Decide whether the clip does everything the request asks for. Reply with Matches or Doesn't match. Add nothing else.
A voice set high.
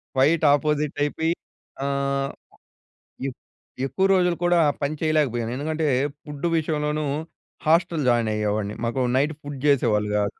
Doesn't match